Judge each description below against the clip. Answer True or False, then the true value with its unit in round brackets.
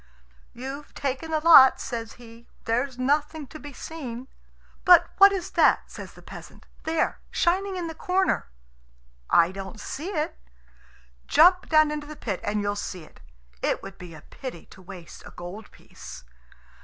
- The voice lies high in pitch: True (270 Hz)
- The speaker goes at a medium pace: True (165 wpm)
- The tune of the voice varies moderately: False (7.3 semitones)